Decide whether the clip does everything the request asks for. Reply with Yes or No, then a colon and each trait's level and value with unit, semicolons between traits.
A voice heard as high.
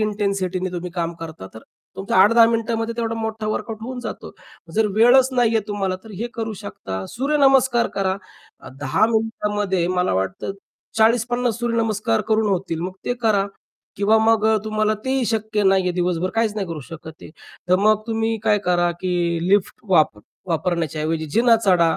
Yes: high, 210 Hz